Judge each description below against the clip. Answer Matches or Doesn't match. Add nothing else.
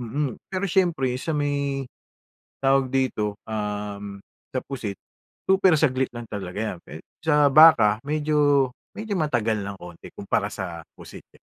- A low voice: Matches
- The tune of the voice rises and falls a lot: Matches